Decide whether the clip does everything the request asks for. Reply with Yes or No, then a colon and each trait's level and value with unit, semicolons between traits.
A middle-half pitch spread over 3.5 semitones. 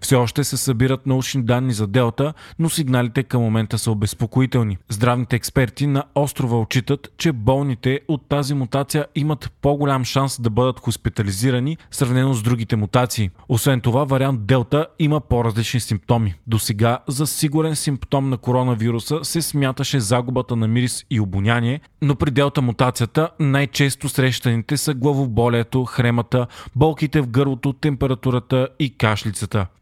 No: average, 3.1 semitones